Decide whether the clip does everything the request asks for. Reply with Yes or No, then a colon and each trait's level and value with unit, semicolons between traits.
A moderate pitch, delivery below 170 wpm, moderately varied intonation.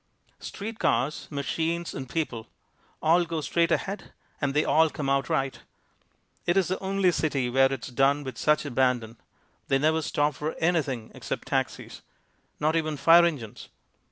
Yes: medium, 150 Hz; average, 155 wpm; average, 3.7 semitones